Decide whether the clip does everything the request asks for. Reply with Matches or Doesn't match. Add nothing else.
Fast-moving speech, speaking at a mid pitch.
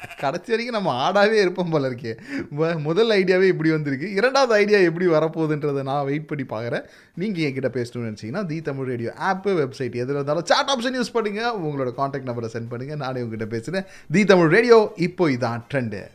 Matches